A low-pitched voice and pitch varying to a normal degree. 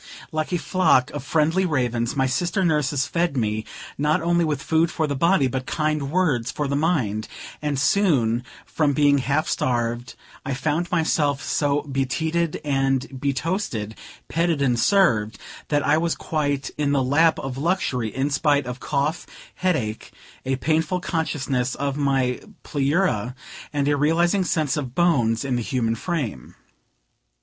No: medium, 145 Hz; average, 3.8 semitones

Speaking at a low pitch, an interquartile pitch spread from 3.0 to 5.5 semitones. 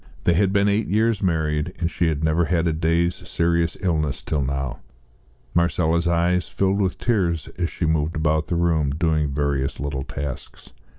No: very low, 85 Hz; narrow, 2.5 semitones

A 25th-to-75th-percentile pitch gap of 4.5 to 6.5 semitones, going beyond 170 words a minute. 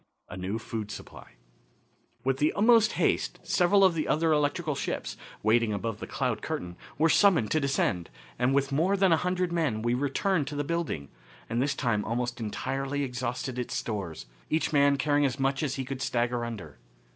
Yes: average, 5.0 semitones; average, 185 wpm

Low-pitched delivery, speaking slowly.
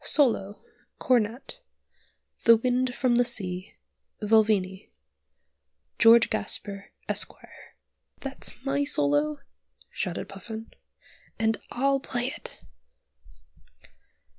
No: high, 225 Hz; slow, 85 wpm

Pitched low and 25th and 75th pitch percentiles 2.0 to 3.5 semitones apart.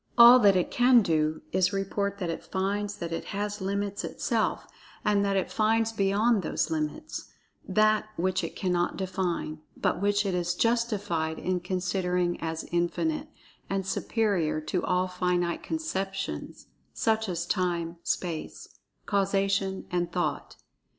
No: high, 190 Hz; average, 2.7 semitones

